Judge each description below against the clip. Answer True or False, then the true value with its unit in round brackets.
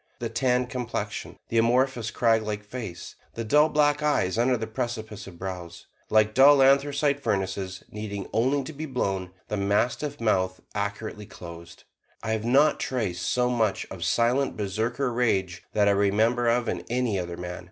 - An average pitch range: True (4.2 semitones)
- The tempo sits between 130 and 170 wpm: True (165 wpm)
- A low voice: True (110 Hz)